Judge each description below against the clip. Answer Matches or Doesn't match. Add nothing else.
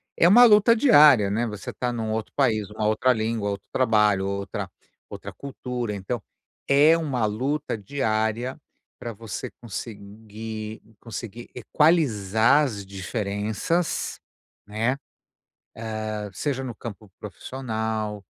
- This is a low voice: Matches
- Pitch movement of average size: Matches